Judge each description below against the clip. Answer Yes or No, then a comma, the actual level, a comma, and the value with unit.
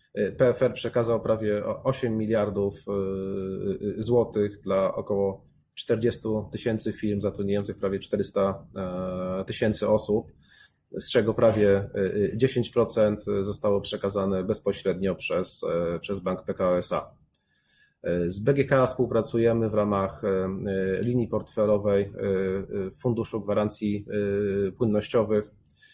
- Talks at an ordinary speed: No, slow, 90 wpm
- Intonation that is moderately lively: No, narrow, 2.3 semitones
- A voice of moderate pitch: No, low, 105 Hz